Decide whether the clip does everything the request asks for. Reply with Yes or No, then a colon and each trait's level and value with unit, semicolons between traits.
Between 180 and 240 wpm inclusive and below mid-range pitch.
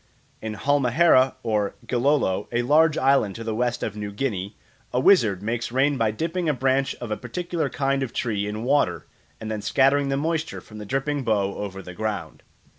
Yes: average, 190 wpm; low, 120 Hz